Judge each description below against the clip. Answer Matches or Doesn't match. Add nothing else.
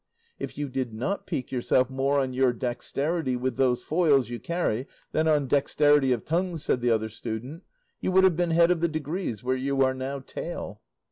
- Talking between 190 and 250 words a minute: Matches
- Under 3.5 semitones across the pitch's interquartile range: Doesn't match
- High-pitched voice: Doesn't match